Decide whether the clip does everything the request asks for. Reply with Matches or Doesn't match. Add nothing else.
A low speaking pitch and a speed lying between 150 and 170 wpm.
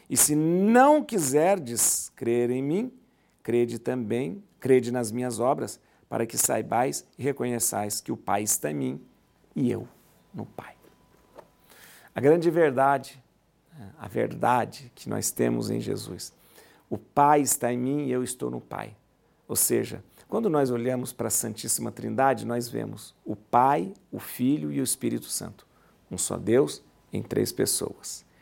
Matches